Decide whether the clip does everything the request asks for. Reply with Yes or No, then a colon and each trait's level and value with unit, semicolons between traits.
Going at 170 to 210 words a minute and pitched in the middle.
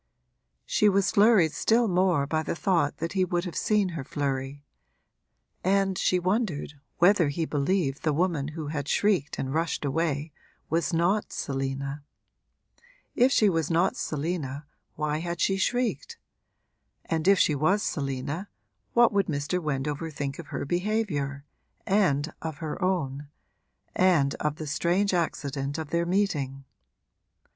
No: average, 145 wpm; medium, 165 Hz